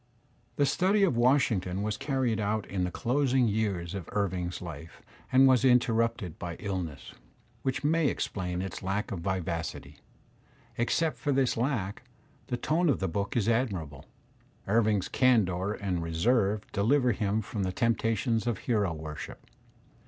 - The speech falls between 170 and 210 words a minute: No, average, 145 wpm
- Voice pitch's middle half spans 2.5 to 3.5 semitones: No, average, 5.2 semitones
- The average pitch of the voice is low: Yes, low, 105 Hz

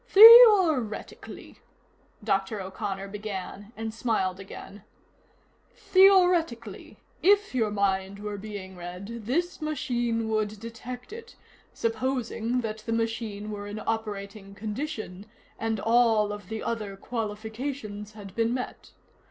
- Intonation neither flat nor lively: Yes, average, 3.1 semitones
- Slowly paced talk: Yes, slow, 115 wpm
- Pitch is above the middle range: Yes, high, 220 Hz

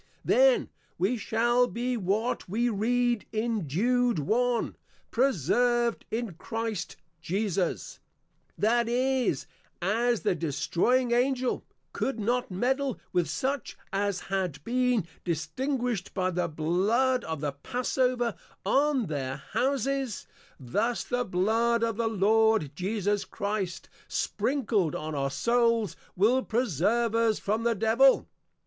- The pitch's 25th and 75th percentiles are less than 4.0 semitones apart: No, average, 4.8 semitones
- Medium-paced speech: No, slow, 115 wpm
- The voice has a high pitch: Yes, high, 225 Hz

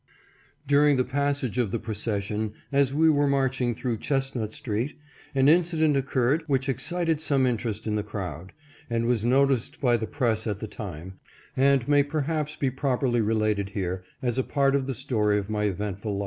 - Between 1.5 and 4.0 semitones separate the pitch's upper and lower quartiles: No, average, 4.7 semitones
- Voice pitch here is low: Yes, low, 125 Hz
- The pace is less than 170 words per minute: No, average, 180 wpm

